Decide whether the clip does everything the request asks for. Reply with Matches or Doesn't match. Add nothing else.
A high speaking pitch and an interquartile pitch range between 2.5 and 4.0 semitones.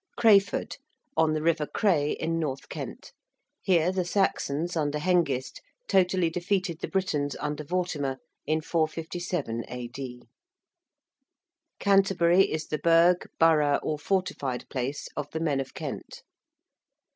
Doesn't match